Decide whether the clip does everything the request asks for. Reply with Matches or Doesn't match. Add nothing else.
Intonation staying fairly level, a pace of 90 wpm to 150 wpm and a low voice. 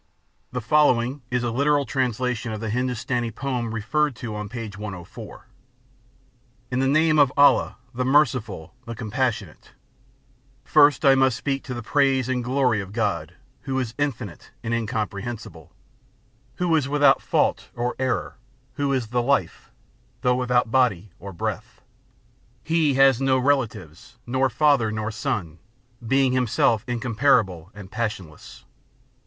Doesn't match